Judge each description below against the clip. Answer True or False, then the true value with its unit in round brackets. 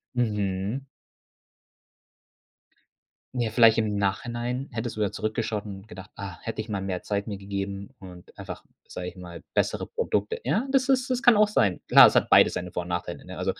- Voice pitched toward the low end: True (105 Hz)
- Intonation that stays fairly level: False (3.6 semitones)